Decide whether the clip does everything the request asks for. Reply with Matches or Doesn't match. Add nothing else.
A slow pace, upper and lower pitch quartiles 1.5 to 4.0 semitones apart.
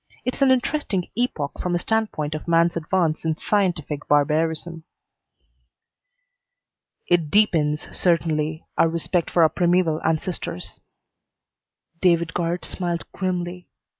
Matches